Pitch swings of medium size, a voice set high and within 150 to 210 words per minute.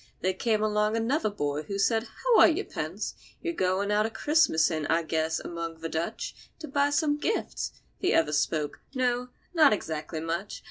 No: wide, 9.0 semitones; high, 210 Hz; average, 175 wpm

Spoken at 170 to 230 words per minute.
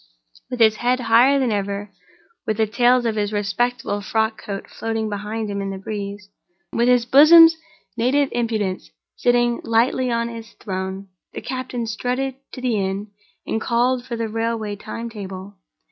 No: average, 160 wpm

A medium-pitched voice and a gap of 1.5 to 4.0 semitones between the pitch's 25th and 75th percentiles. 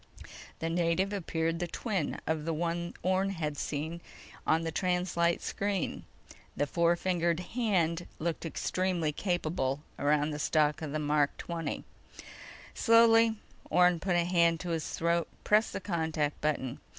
Yes: medium, 170 Hz; narrow, 2.5 semitones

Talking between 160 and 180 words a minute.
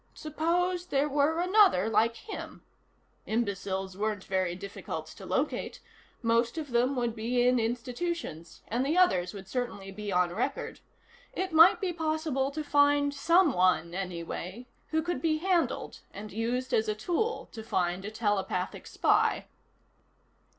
No: average, 145 wpm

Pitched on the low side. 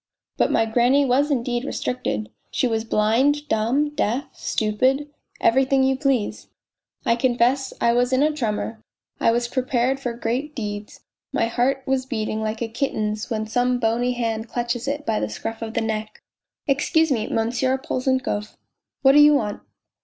No: high, 245 Hz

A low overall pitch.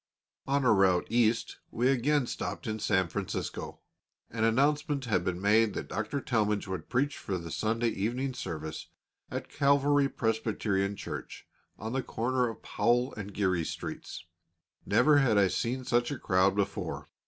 Yes: low, 115 Hz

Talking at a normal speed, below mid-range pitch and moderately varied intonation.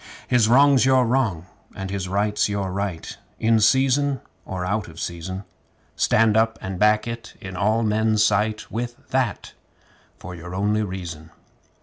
Yes: average, 150 wpm; low, 105 Hz; average, 3.4 semitones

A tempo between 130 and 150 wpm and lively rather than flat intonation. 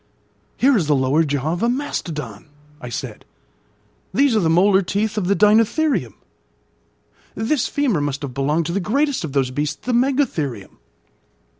No: average, 160 wpm; wide, 8.5 semitones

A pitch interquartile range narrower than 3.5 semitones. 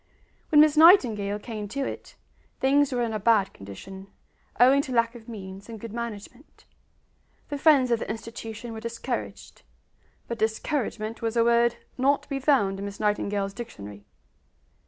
No: average, 3.8 semitones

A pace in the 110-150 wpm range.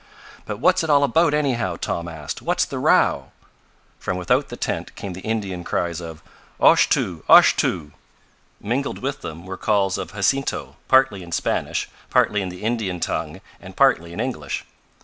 No: average, 165 wpm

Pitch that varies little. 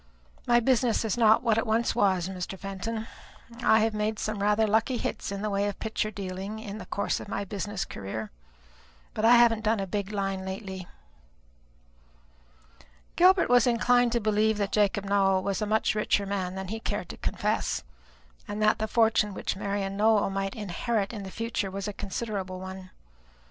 Yes: narrow, 2.2 semitones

